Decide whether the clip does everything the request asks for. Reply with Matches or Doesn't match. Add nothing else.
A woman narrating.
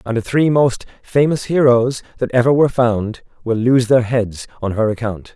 Doesn't match